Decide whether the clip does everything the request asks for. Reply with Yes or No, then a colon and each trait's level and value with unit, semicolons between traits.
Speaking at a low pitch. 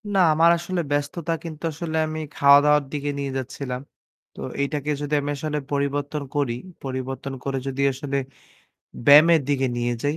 No: medium, 145 Hz